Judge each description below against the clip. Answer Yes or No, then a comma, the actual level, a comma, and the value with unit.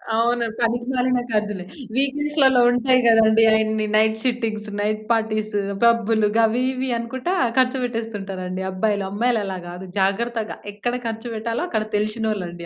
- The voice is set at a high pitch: Yes, high, 225 Hz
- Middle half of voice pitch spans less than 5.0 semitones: Yes, narrow, 2.4 semitones